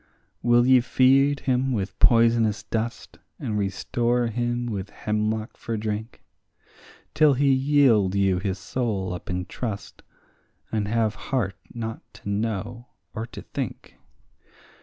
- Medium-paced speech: No, slow, 130 wpm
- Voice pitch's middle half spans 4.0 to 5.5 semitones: No, average, 2.8 semitones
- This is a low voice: Yes, low, 115 Hz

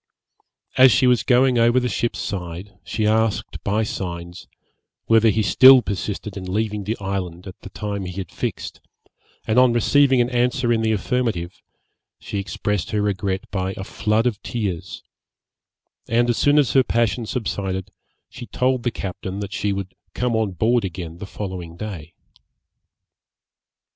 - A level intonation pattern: No, average, 3.9 semitones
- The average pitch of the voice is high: No, low, 105 Hz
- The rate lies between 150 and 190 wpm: Yes, average, 160 wpm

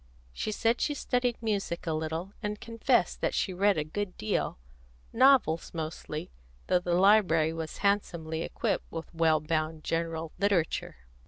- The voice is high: No, medium, 170 Hz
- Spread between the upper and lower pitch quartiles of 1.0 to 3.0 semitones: No, average, 4.4 semitones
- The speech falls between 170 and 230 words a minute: No, average, 150 wpm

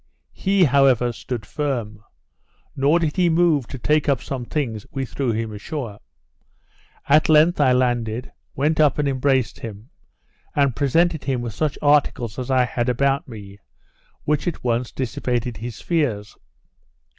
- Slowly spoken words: No, average, 150 wpm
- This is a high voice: No, low, 130 Hz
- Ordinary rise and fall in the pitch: Yes, average, 4.0 semitones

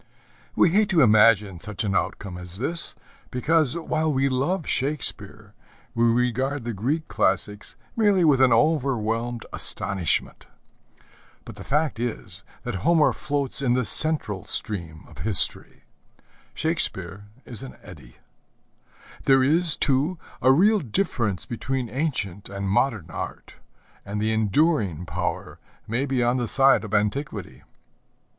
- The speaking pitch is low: Yes, low, 120 Hz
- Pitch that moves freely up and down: Yes, wide, 6.1 semitones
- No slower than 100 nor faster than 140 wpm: Yes, slow, 135 wpm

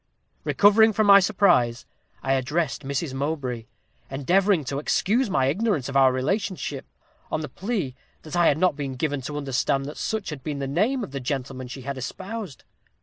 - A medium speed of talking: Yes, average, 180 wpm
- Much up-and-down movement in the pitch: Yes, wide, 6.3 semitones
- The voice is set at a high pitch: No, medium, 145 Hz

